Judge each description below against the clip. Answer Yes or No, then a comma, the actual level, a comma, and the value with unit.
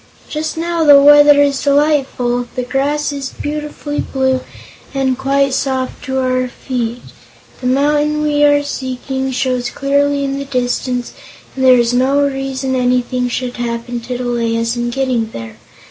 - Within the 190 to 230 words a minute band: No, average, 155 wpm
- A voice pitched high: Yes, very high, 265 Hz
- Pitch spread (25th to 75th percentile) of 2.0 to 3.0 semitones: Yes, narrow, 2.4 semitones